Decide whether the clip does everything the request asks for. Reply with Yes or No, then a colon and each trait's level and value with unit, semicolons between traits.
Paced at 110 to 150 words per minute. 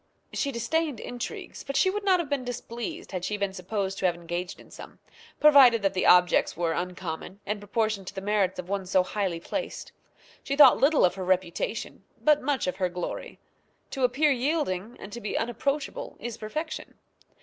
No: average, 190 wpm